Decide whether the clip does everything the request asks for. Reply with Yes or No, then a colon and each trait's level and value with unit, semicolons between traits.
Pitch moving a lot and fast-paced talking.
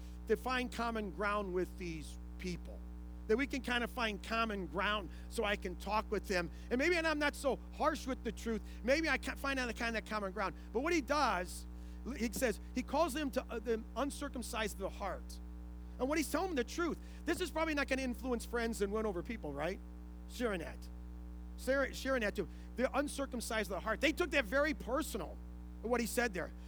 Yes: wide, 7.3 semitones; fast, 215 wpm